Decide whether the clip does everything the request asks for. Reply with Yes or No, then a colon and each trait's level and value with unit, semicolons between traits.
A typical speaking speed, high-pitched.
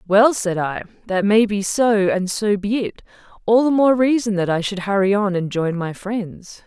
No: fast, 215 wpm; high, 205 Hz